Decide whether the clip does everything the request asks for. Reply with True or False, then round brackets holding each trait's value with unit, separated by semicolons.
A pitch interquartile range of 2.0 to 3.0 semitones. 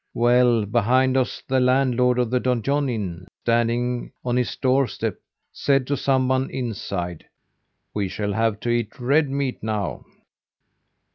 True (2.7 semitones)